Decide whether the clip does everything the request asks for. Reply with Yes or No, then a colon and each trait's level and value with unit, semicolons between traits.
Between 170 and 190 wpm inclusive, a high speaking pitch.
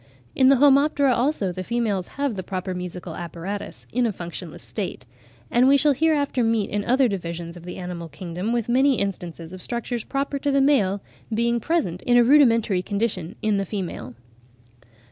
Yes: average, 180 wpm; high, 215 Hz